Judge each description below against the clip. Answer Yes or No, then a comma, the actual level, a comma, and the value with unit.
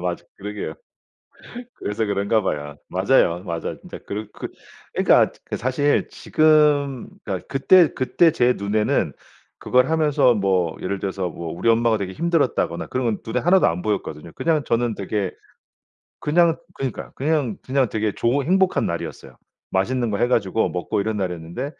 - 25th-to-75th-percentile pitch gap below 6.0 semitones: No, wide, 6.4 semitones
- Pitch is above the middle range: No, low, 110 Hz